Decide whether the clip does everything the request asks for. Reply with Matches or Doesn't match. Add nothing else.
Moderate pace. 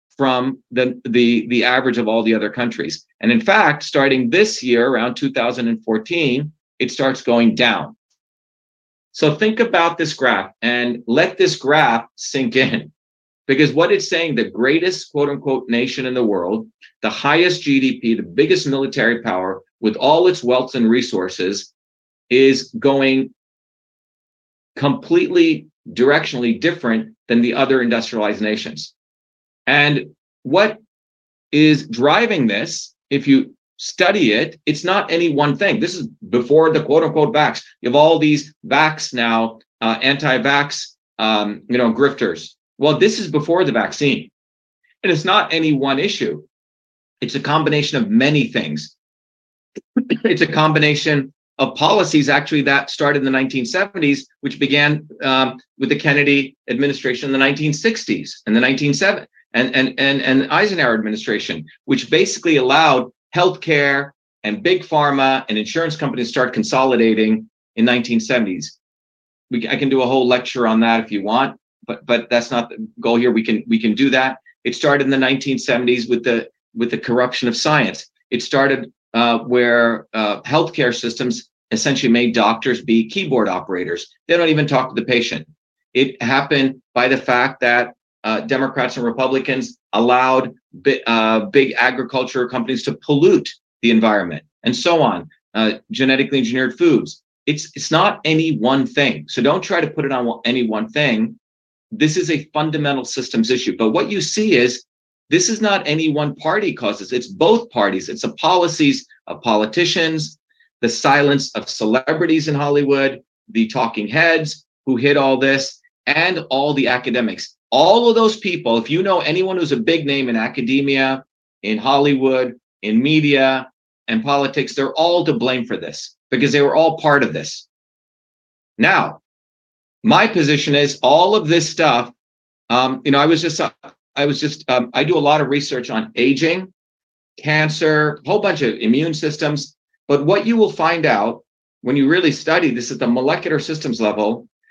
Matches